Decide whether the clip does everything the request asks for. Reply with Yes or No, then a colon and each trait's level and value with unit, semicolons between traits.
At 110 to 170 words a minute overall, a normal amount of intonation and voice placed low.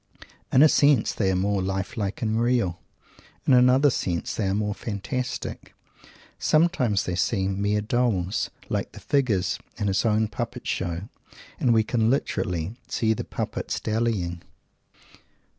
Yes: average, 145 wpm; average, 4.2 semitones; low, 110 Hz